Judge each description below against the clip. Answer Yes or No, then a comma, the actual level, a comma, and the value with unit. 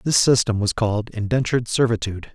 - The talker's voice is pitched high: No, low, 115 Hz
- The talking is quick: No, average, 155 wpm